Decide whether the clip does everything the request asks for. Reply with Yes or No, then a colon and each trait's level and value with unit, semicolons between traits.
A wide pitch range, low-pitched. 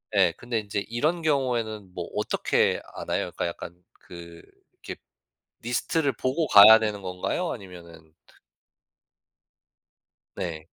Yes: wide, 5.9 semitones; low, 105 Hz